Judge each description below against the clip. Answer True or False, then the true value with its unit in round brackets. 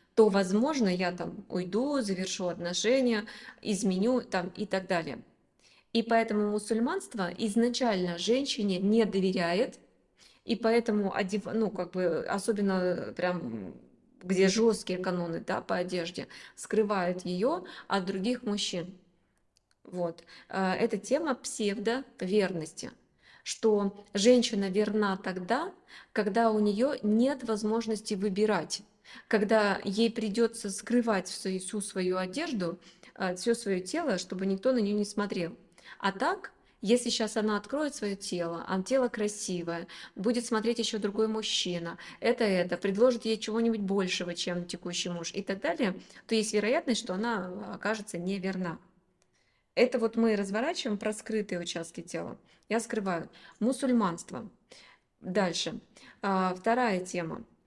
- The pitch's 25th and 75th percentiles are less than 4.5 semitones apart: True (3.7 semitones)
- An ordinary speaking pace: True (120 wpm)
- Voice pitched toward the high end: True (210 Hz)